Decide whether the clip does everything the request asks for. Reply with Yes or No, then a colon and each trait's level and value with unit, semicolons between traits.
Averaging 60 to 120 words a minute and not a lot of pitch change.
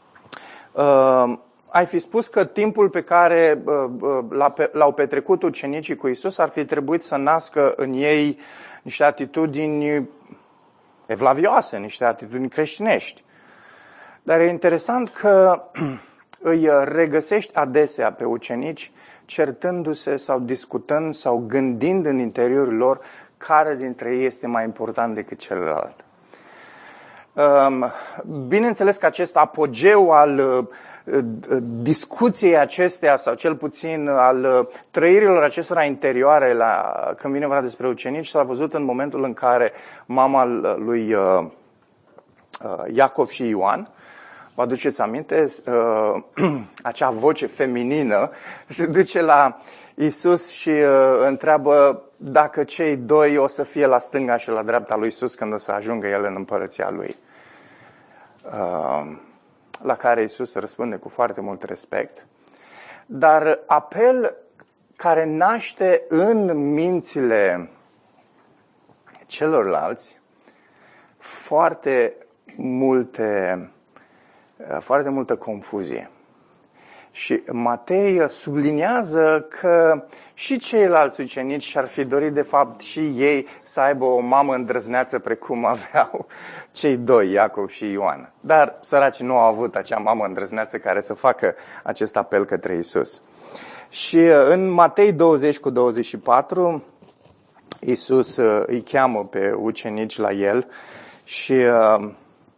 No: slow, 115 wpm; average, 4.4 semitones